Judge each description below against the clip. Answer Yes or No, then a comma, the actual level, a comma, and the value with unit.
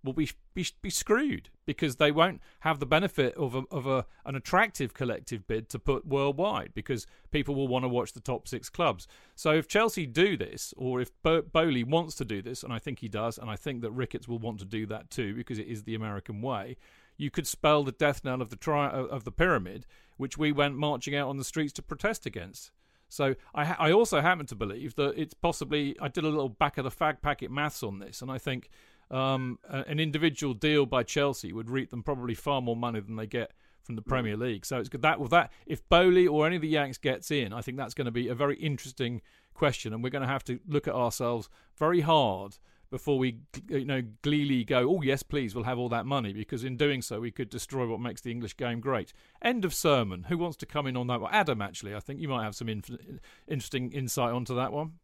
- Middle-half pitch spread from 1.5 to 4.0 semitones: Yes, average, 3.7 semitones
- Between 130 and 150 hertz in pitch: Yes, low, 135 Hz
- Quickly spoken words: Yes, fast, 240 wpm